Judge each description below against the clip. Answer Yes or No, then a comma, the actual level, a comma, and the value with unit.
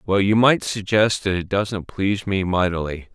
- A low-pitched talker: Yes, low, 100 Hz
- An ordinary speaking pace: Yes, average, 190 wpm